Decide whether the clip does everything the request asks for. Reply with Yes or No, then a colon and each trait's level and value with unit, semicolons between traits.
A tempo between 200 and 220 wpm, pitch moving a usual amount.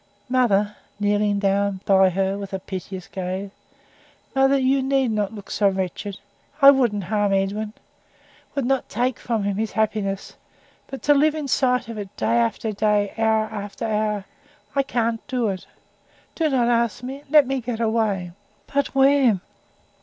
No: average, 160 wpm; average, 4.4 semitones